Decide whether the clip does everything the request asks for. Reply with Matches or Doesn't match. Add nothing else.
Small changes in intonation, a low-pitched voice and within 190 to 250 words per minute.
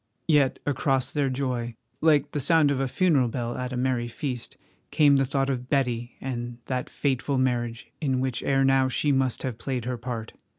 Matches